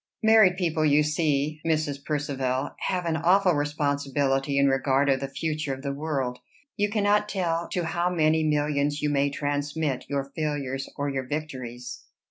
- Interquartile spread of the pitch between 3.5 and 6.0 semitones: No, narrow, 2.5 semitones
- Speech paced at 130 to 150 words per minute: No, average, 160 wpm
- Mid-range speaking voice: Yes, medium, 145 Hz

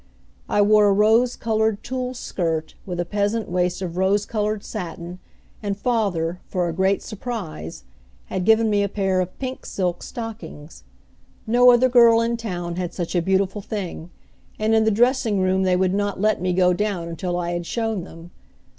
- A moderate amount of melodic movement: Yes, average, 3.7 semitones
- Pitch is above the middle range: Yes, high, 200 Hz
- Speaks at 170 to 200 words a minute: Yes, average, 180 wpm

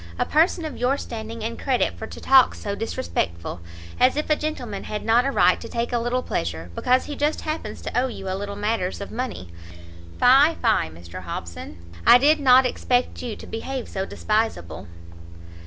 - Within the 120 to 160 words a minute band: No, average, 190 wpm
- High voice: Yes, high, 235 Hz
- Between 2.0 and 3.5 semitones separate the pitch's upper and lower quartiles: No, average, 5.0 semitones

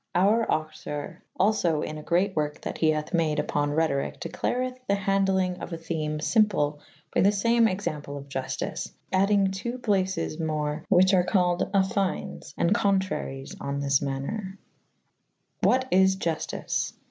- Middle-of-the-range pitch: Yes, medium, 180 Hz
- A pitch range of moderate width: Yes, average, 4.5 semitones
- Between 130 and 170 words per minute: Yes, average, 160 wpm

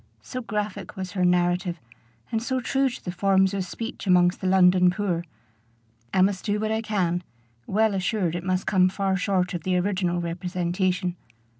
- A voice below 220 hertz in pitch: Yes, medium, 185 Hz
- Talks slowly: No, average, 175 wpm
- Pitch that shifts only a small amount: Yes, narrow, 2.3 semitones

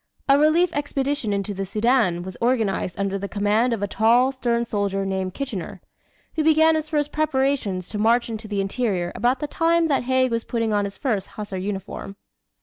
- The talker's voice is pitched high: Yes, high, 230 Hz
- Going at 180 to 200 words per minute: Yes, average, 190 wpm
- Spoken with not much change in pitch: No, wide, 5.5 semitones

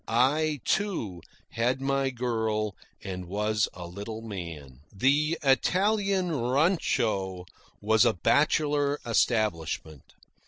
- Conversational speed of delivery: No, slow, 95 wpm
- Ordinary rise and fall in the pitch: No, wide, 6.7 semitones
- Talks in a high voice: No, low, 115 Hz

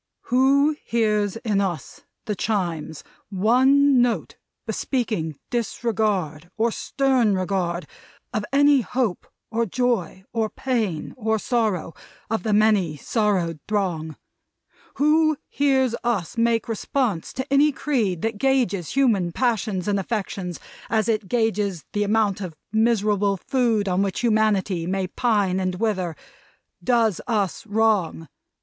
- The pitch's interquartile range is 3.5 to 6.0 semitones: Yes, average, 4.1 semitones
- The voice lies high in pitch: Yes, high, 215 Hz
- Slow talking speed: Yes, slow, 125 wpm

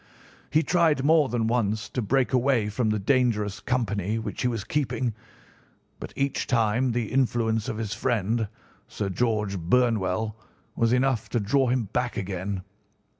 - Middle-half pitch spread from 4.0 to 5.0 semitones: No, average, 3.2 semitones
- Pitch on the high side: No, low, 115 Hz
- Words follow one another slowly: No, average, 155 wpm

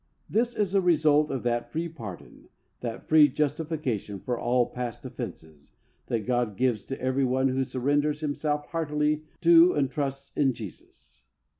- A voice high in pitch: No, low, 135 Hz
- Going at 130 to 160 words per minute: Yes, average, 155 wpm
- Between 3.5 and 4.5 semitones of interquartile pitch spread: Yes, average, 3.9 semitones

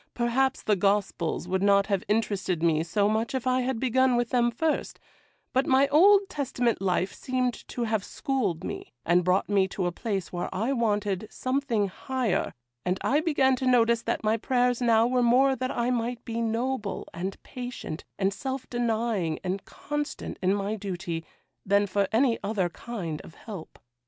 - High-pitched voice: Yes, high, 225 Hz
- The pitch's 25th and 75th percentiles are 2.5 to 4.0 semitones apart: No, average, 4.6 semitones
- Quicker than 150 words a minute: Yes, average, 175 wpm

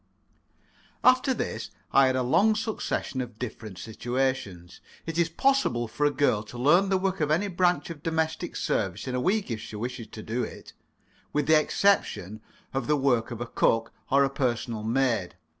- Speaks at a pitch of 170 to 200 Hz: No, low, 135 Hz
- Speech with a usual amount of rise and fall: No, wide, 6.3 semitones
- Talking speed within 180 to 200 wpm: Yes, average, 185 wpm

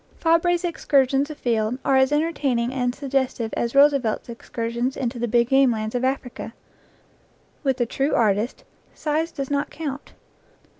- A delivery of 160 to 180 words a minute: No, average, 145 wpm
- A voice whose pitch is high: Yes, very high, 265 Hz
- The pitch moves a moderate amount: Yes, average, 3.2 semitones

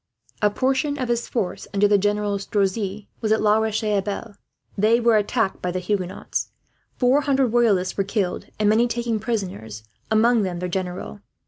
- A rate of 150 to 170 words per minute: Yes, average, 165 wpm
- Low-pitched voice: No, high, 210 Hz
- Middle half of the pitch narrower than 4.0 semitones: Yes, average, 3.2 semitones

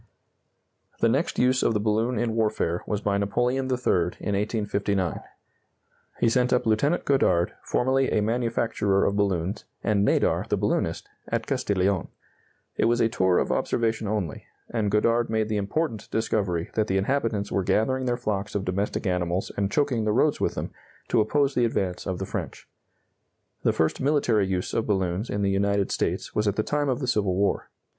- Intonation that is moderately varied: Yes, average, 3.4 semitones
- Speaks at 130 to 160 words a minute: No, average, 180 wpm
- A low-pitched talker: Yes, low, 105 Hz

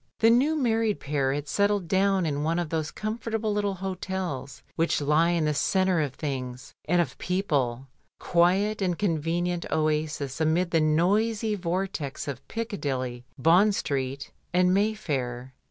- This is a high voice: No, medium, 170 Hz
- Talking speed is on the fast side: No, average, 145 wpm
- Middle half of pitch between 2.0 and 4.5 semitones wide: No, wide, 5.5 semitones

